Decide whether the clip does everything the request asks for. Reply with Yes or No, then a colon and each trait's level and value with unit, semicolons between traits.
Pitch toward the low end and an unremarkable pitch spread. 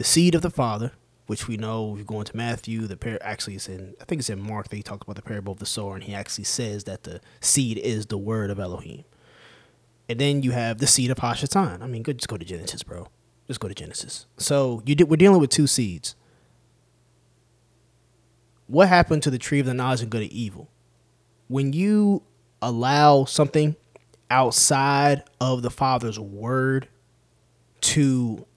Yes: low, 120 Hz; average, 4.0 semitones